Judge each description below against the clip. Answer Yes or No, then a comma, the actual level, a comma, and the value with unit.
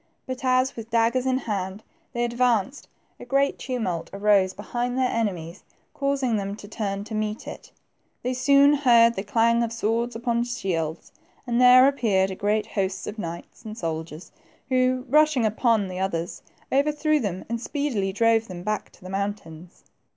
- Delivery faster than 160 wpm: Yes, average, 170 wpm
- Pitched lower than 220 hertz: No, high, 225 Hz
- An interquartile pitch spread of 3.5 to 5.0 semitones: Yes, average, 4.4 semitones